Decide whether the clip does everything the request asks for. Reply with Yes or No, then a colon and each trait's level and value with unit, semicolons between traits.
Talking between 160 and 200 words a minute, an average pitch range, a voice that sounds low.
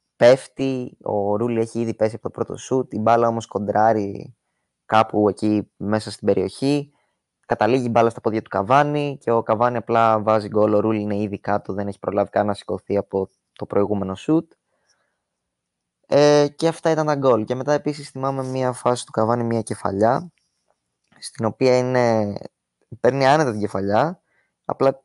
Yes: fast, 170 wpm; average, 4.0 semitones; low, 115 Hz